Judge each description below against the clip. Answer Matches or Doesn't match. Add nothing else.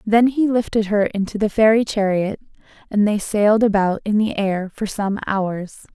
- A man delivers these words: Doesn't match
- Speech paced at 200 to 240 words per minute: Doesn't match